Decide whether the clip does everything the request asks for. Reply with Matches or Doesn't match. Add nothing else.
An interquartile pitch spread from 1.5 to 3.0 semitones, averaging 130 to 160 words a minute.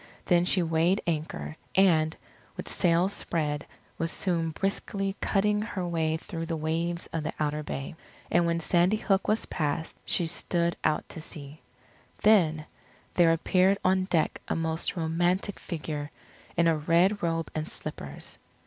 Matches